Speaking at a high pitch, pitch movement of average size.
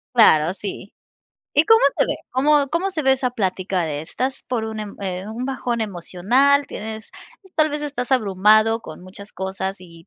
No: high, 220 Hz; wide, 5.9 semitones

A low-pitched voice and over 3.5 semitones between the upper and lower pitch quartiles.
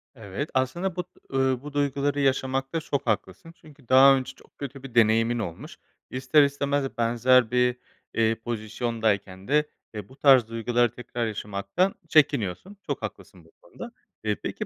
Yes: low, 130 Hz; average, 3.9 semitones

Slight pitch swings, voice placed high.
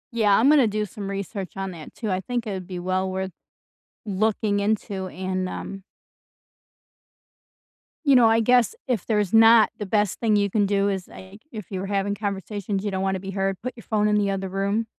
Yes: narrow, 2.2 semitones; high, 200 Hz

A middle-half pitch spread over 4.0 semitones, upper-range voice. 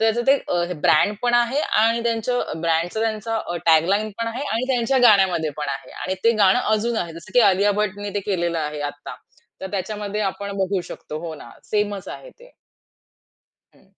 Yes: average, 4.7 semitones; high, 205 Hz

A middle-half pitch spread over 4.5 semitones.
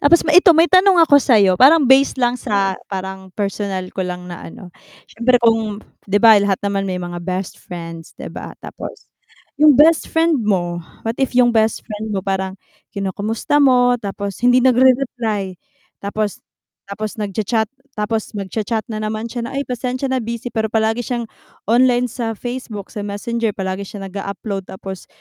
No: average, 4.0 semitones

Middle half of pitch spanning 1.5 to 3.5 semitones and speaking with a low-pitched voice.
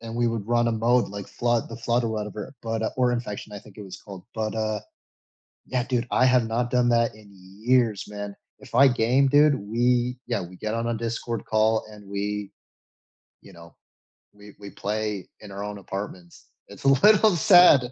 Yes: average, 2.9 semitones; low, 115 Hz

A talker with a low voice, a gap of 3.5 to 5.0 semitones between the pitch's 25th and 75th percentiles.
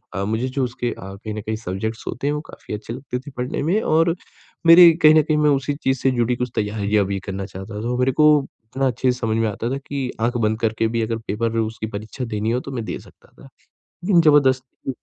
Yes: low, 120 Hz; average, 3.9 semitones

